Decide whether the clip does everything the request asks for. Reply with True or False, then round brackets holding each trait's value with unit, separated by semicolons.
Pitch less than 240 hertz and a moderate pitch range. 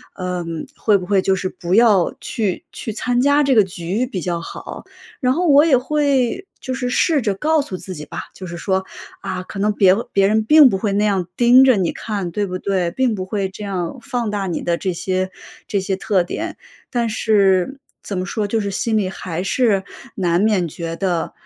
True (200 Hz; 4.3 semitones)